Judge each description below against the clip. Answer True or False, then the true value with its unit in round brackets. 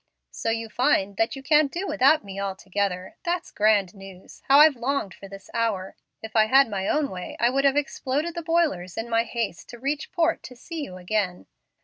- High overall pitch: True (230 Hz)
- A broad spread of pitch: True (6.4 semitones)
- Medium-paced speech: False (210 wpm)